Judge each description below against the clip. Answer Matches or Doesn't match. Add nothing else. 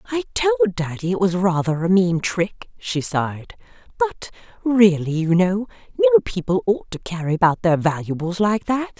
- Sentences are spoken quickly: Doesn't match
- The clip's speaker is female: Matches